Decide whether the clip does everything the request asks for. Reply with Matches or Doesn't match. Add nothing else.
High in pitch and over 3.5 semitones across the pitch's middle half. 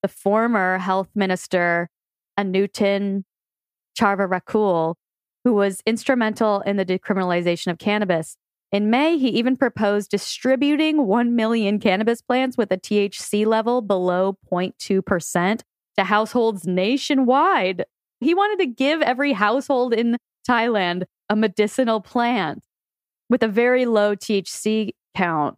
Matches